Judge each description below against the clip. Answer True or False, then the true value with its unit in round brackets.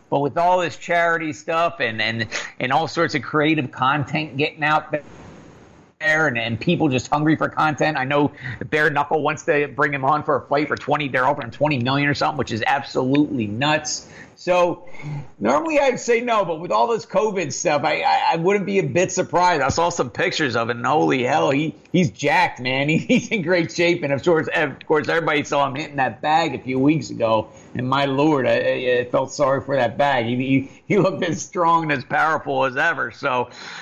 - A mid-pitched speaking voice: True (150 Hz)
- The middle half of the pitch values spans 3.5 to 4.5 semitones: True (3.8 semitones)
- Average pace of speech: False (220 wpm)